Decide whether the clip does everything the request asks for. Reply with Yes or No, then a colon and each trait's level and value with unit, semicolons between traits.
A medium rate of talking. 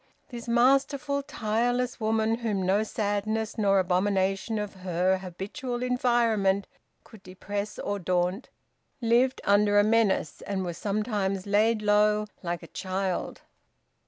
No: slow, 125 wpm